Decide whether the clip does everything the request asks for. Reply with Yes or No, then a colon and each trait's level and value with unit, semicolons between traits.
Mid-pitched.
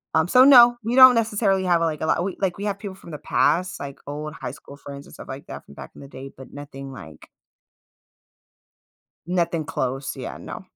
Yes: medium, 165 Hz